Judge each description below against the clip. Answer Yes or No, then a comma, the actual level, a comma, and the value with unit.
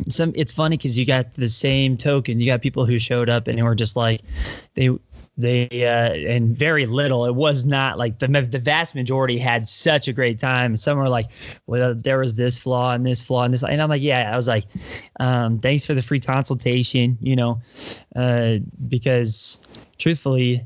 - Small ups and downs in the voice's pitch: Yes, narrow, 2.1 semitones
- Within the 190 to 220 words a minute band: Yes, fast, 205 wpm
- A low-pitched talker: Yes, low, 125 Hz